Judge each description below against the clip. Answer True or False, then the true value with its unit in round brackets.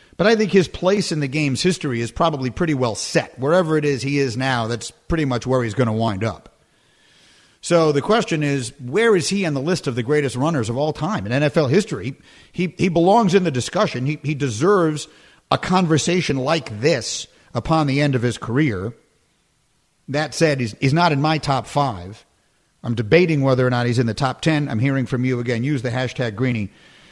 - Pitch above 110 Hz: True (140 Hz)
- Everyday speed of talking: False (210 wpm)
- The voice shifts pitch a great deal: False (4.6 semitones)